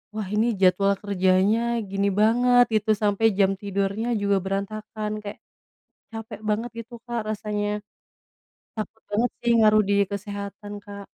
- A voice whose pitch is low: No, high, 210 Hz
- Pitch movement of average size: No, narrow, 1.9 semitones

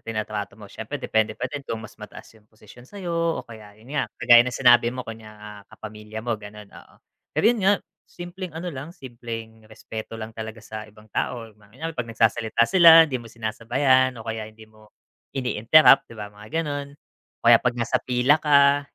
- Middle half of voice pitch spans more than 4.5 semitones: No, average, 4.2 semitones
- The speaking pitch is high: No, low, 115 Hz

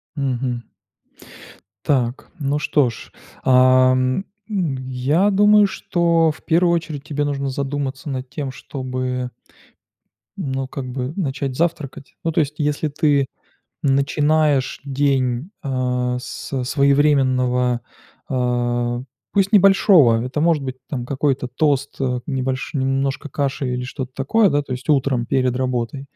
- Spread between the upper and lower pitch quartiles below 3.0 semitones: Yes, narrow, 2.6 semitones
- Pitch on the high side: No, low, 135 Hz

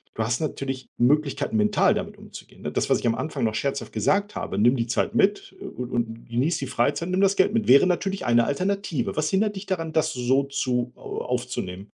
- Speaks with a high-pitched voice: No, medium, 140 Hz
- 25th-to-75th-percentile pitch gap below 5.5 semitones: No, wide, 7.3 semitones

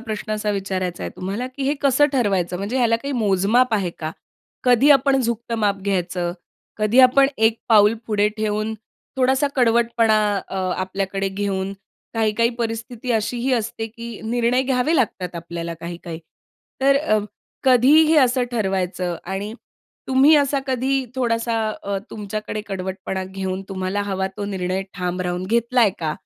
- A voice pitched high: Yes, high, 215 Hz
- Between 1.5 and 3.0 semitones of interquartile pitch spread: No, average, 4.4 semitones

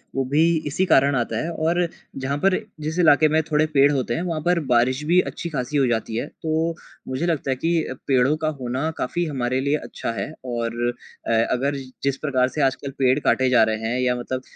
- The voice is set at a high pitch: No, medium, 140 Hz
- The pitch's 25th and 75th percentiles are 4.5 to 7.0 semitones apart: No, average, 3.7 semitones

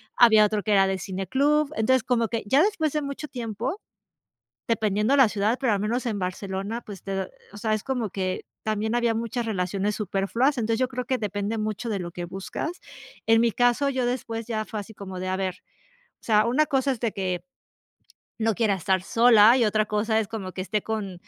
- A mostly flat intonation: No, average, 3.4 semitones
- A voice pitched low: No, high, 220 Hz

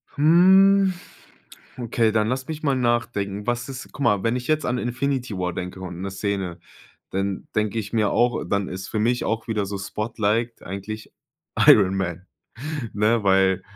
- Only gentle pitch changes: No, average, 4.0 semitones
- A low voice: Yes, low, 110 Hz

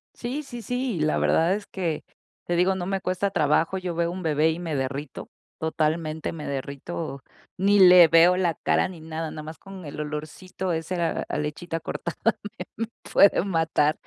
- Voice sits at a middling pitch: Yes, medium, 170 Hz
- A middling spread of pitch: Yes, average, 3.2 semitones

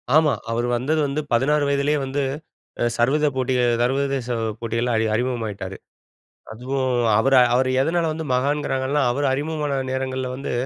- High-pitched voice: No, low, 130 Hz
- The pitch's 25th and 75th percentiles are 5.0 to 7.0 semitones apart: No, average, 2.9 semitones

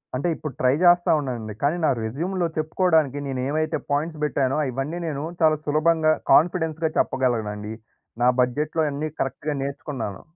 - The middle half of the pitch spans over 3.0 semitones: Yes, average, 3.4 semitones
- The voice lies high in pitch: No, medium, 150 Hz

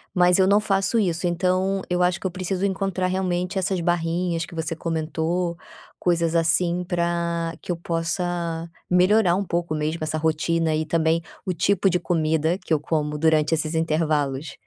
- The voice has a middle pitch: Yes, medium, 170 Hz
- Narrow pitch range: Yes, narrow, 2.1 semitones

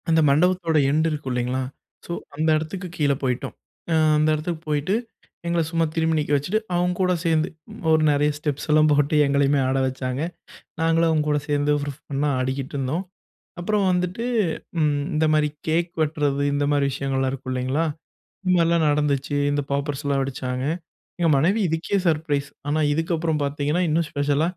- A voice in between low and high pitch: Yes, medium, 150 Hz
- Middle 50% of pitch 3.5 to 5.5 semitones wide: No, narrow, 2.6 semitones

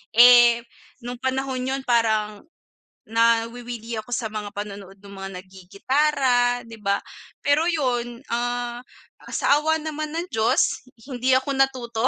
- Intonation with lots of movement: No, average, 2.9 semitones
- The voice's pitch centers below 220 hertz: No, high, 240 Hz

